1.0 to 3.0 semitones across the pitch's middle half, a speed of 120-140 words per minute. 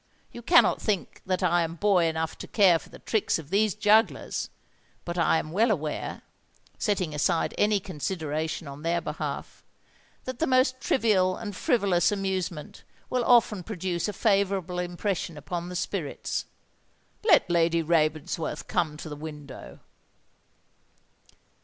No: average, 4.3 semitones; slow, 135 wpm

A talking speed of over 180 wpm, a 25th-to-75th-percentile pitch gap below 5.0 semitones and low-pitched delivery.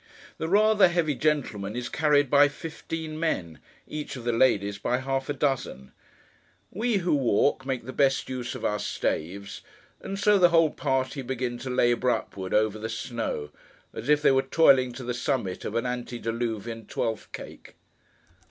No: average, 165 wpm; average, 4.5 semitones; low, 130 Hz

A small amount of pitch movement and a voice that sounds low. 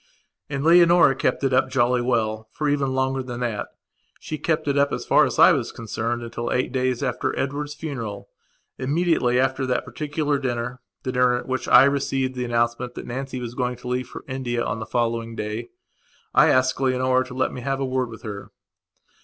Yes: narrow, 2.1 semitones; low, 130 Hz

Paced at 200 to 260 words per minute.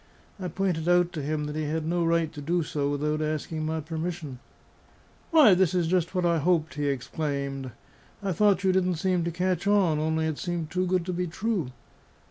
Yes: fast, 205 wpm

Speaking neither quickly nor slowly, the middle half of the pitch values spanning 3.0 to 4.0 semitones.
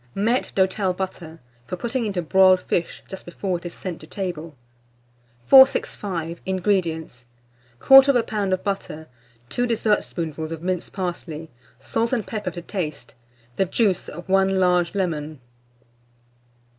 No: slow, 130 wpm; average, 3.4 semitones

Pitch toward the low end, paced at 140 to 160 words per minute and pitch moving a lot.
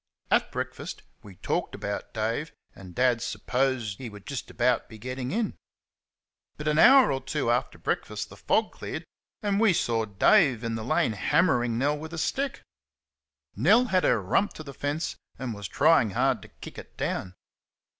No: low, 125 Hz; average, 175 wpm; wide, 5.9 semitones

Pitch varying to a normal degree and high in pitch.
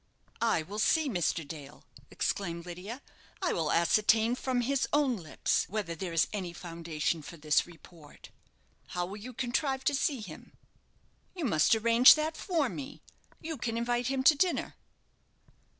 No: wide, 7.7 semitones; high, 220 Hz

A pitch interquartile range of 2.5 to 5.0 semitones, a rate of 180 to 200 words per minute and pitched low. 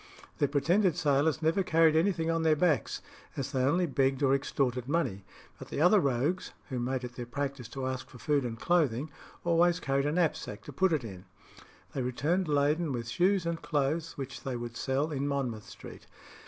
No: average, 4.1 semitones; average, 195 wpm; medium, 145 Hz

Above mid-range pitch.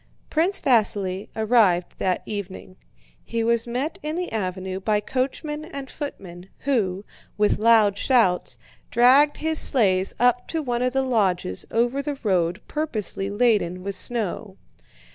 Yes: high, 225 Hz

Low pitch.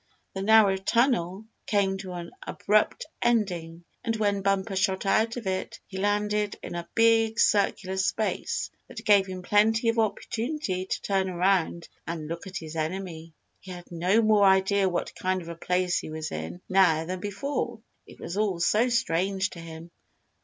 No: high, 190 Hz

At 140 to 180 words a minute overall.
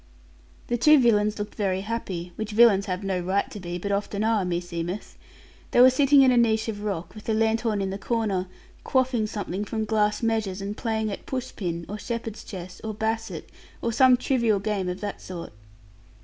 No: average, 195 wpm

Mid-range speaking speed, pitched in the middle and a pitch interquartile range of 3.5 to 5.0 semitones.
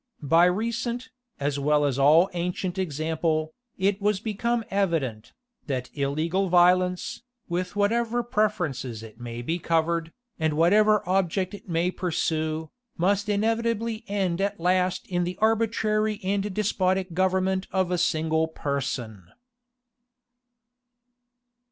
No: slow, 120 wpm; medium, 180 Hz; average, 4.3 semitones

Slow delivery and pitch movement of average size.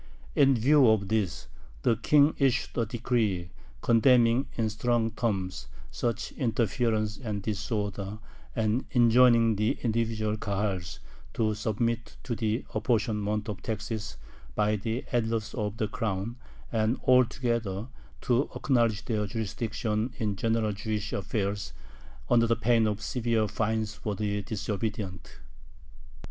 No: slow, 125 wpm; narrow, 1.9 semitones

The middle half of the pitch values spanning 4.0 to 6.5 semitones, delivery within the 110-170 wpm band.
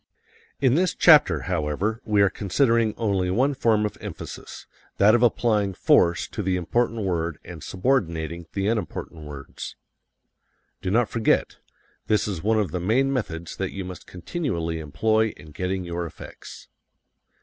Yes: average, 4.7 semitones; average, 150 wpm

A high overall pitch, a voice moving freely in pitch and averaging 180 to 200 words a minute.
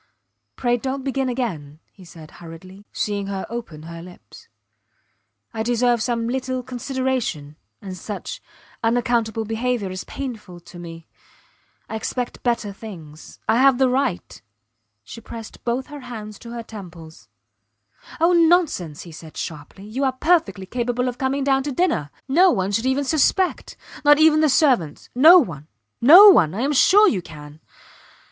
No: high, 235 Hz; wide, 6.2 semitones; average, 155 wpm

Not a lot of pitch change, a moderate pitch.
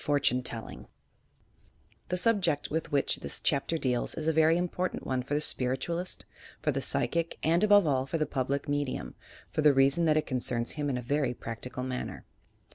No: average, 4.1 semitones; medium, 145 Hz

